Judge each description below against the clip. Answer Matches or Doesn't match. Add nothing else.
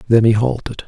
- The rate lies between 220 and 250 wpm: Doesn't match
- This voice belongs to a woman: Doesn't match